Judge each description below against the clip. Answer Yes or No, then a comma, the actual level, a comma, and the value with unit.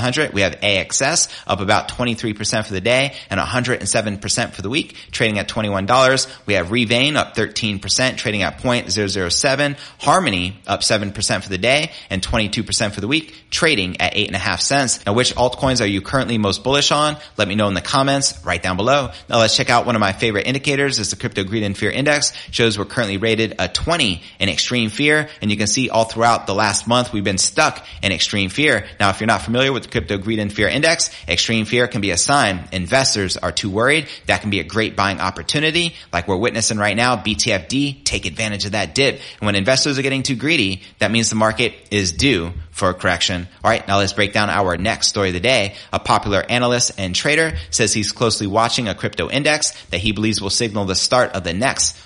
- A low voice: Yes, low, 110 Hz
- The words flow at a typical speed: No, fast, 235 wpm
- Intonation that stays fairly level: No, average, 4.0 semitones